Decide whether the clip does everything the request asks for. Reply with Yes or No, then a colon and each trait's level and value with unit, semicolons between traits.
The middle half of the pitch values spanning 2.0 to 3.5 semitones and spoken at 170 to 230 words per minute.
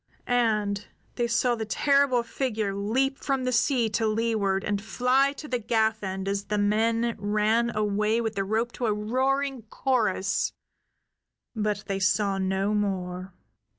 No: average, 3.1 semitones; average, 150 wpm